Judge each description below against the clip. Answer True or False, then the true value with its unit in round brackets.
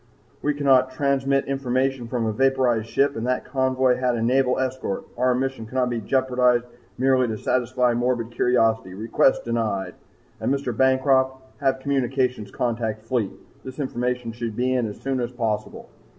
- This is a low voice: True (125 Hz)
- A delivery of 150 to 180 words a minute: True (160 wpm)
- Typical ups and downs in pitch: False (2.0 semitones)